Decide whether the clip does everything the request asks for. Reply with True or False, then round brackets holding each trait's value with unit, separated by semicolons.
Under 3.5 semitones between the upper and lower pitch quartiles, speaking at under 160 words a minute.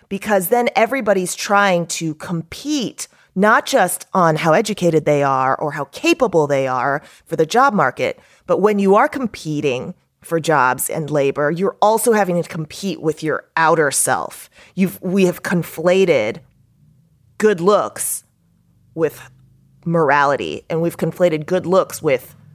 False (5.2 semitones; 140 wpm)